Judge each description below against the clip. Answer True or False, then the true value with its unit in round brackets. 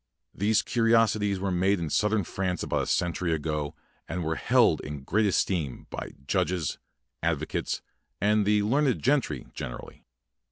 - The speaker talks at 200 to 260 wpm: False (150 wpm)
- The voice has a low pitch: True (95 Hz)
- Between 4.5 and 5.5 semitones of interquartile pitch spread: True (4.8 semitones)